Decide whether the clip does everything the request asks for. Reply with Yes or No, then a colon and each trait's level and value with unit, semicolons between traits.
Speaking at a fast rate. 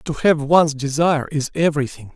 No: average, 165 wpm